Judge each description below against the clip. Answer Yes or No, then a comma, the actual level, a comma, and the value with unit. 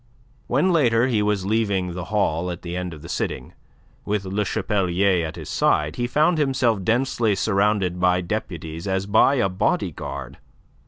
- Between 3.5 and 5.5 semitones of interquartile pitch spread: Yes, average, 4.0 semitones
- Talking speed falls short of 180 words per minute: Yes, average, 170 wpm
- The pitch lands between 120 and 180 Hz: No, low, 100 Hz